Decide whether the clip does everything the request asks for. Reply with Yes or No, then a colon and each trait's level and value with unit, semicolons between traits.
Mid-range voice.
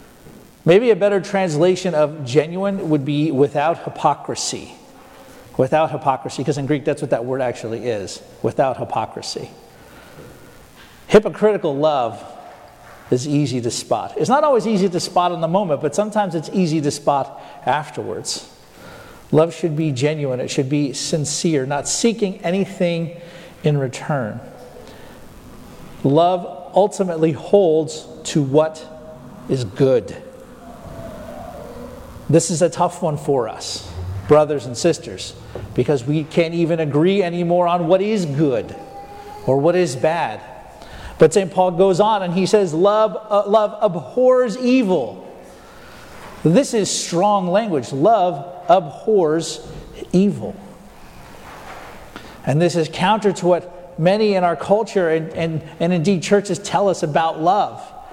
Yes: medium, 170 Hz